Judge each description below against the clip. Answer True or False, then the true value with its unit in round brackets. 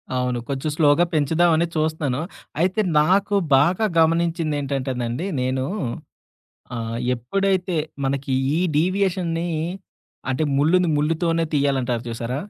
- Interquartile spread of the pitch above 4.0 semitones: True (4.6 semitones)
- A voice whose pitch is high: False (155 Hz)